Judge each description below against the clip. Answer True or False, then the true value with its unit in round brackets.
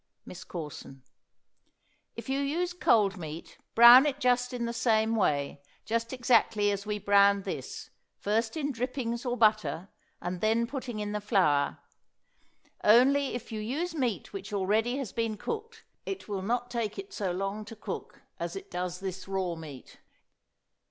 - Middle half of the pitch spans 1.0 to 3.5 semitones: False (4.3 semitones)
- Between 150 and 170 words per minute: True (160 wpm)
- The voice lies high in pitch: True (225 Hz)